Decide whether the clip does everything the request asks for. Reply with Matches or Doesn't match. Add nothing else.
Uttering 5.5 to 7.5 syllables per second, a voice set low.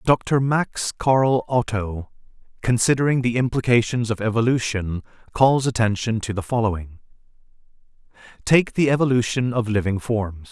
Doesn't match